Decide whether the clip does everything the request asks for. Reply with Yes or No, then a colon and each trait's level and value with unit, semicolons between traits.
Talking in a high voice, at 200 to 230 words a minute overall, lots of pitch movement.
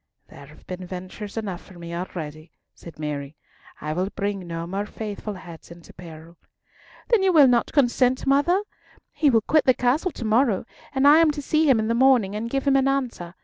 Yes: high, 210 Hz; fast, 205 wpm; wide, 7.5 semitones